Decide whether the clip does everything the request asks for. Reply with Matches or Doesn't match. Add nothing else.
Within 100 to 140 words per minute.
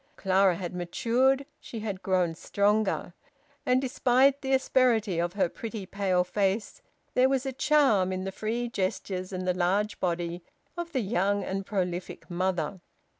Doesn't match